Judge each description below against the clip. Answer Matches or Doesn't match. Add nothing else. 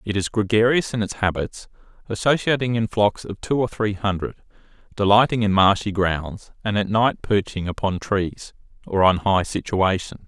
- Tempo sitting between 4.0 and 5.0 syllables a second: Matches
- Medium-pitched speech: Doesn't match